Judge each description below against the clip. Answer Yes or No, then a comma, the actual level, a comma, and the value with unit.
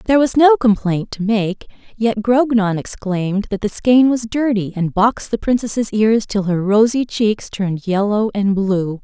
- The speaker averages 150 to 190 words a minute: Yes, average, 180 wpm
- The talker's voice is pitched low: No, high, 215 Hz